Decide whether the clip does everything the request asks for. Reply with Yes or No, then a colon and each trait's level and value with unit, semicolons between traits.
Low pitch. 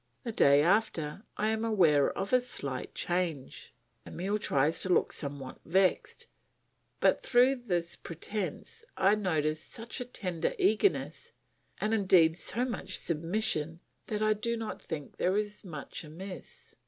No: high, 190 Hz